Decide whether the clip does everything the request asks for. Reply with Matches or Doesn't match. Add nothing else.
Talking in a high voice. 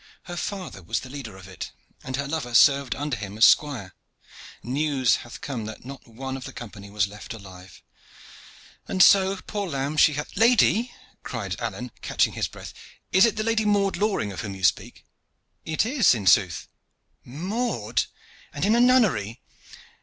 Doesn't match